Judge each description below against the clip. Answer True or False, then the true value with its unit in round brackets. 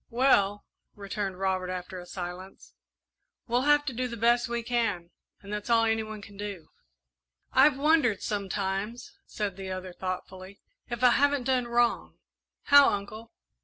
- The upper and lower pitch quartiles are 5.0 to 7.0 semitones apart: False (4.0 semitones)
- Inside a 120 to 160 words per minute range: True (155 wpm)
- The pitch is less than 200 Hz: False (210 Hz)